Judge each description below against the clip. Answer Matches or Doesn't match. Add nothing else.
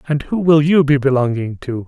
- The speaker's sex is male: Matches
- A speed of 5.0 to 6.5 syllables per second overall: Matches